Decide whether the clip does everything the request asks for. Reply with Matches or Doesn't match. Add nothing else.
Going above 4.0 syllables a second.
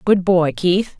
Doesn't match